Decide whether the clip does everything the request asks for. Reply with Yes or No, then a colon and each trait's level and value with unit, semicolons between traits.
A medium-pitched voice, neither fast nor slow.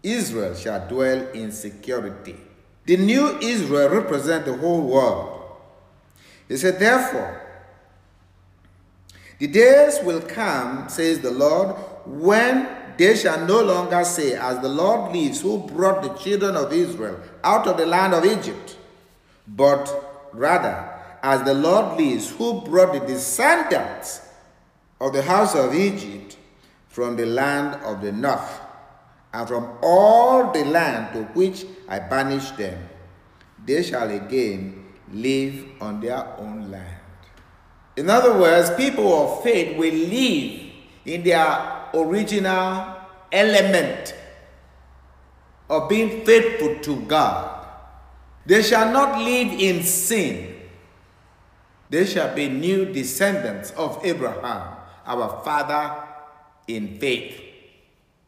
No: medium, 150 Hz; slow, 120 wpm